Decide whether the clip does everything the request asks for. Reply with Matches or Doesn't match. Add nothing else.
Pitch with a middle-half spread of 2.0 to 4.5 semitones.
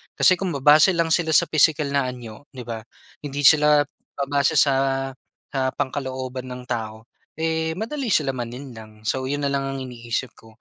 Matches